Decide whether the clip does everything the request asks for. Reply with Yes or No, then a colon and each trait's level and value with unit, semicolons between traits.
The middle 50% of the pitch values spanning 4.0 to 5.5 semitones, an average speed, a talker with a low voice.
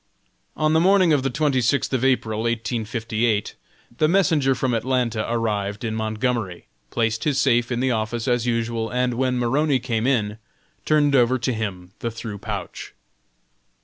No: average, 2.9 semitones; average, 160 wpm; low, 120 Hz